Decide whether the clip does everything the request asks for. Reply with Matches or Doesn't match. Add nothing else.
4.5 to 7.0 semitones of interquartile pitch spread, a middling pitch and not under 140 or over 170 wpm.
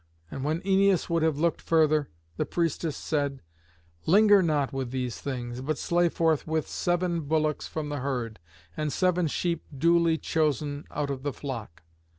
Doesn't match